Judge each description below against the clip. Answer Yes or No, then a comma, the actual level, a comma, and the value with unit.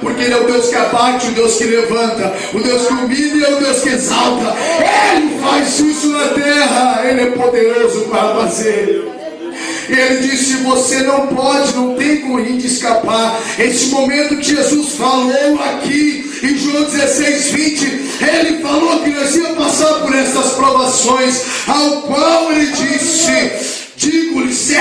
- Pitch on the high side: Yes, very high, 270 Hz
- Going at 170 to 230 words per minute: No, average, 155 wpm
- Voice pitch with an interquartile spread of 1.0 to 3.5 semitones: Yes, average, 2.8 semitones